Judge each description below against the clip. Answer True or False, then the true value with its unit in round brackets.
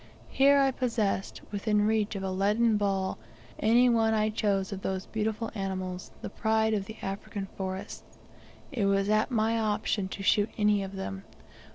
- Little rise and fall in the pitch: True (2.3 semitones)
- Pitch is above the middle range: True (210 Hz)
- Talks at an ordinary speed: True (170 wpm)